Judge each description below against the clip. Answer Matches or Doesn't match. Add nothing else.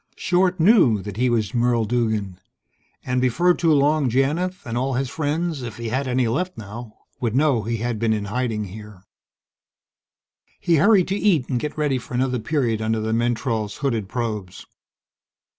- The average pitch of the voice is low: Matches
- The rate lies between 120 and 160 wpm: Doesn't match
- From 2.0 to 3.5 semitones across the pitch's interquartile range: Doesn't match